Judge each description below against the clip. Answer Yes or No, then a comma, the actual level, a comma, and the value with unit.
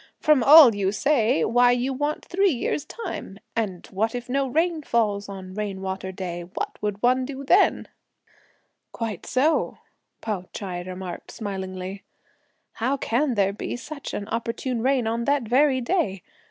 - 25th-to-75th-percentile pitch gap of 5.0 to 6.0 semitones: Yes, wide, 5.6 semitones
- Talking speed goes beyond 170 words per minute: No, average, 155 wpm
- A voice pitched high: Yes, high, 230 Hz